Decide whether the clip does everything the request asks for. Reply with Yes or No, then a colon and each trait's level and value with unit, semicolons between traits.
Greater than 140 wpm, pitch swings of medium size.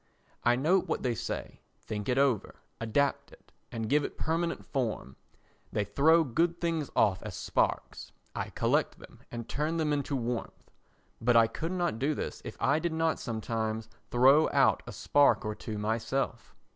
No: average, 170 wpm; wide, 5.7 semitones